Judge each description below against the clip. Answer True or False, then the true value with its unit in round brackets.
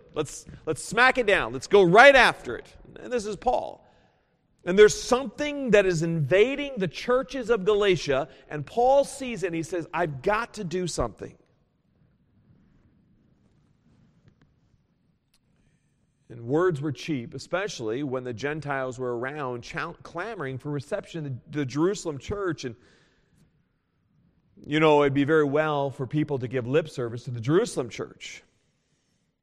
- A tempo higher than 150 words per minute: False (145 wpm)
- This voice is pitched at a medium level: True (160 Hz)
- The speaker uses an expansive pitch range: True (6.9 semitones)